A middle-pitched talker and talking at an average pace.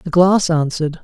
Yes: medium, 165 Hz; average, 175 wpm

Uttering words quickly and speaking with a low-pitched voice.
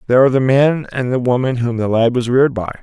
Yes: fast, 275 wpm; low, 125 Hz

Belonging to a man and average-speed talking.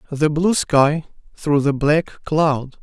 Yes: male; average, 150 wpm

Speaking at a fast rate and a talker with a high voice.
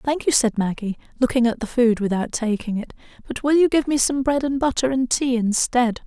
Yes: fast, 225 wpm; high, 245 Hz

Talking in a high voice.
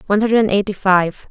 Yes: high, 200 Hz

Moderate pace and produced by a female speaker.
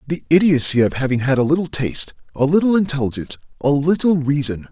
No: average, 180 wpm; male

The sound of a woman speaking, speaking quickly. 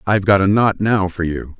No: male; fast, 265 wpm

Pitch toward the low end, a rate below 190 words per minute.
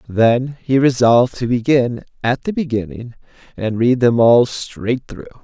Yes: low, 120 Hz; average, 155 wpm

